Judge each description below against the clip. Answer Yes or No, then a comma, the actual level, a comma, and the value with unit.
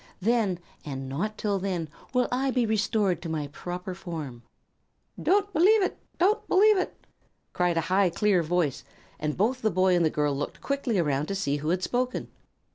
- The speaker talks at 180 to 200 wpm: Yes, average, 185 wpm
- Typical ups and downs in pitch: No, wide, 6.9 semitones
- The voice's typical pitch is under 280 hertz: Yes, medium, 185 Hz